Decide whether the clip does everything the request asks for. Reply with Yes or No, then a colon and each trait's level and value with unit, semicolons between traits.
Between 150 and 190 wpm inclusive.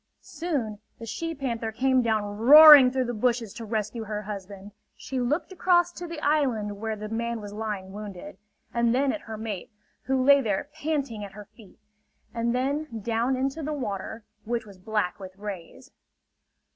Yes: average, 175 wpm